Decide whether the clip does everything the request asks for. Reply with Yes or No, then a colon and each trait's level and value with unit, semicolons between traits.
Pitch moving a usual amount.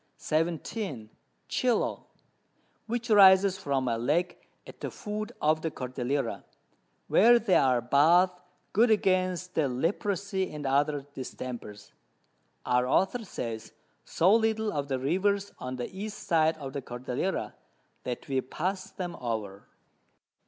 No: wide, 7.1 semitones